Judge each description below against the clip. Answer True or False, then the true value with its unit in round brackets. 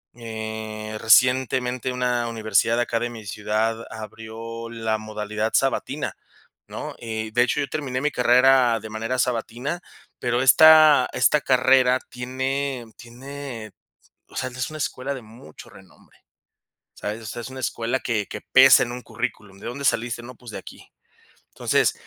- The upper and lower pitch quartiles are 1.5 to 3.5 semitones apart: True (2.7 semitones)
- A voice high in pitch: False (120 Hz)